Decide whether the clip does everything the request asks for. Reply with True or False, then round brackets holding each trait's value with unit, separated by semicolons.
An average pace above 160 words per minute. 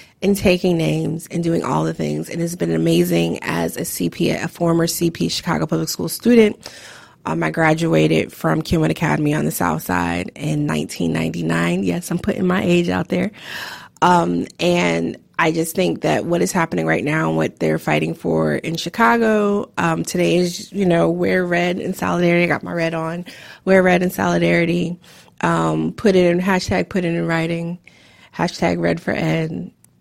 True (180 wpm)